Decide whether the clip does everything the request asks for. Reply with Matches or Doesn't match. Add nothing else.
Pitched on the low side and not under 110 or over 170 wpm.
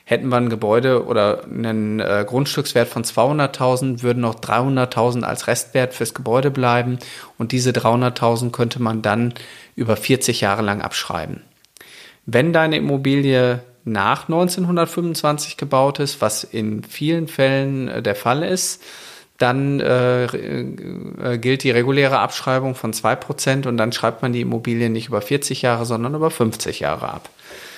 Matches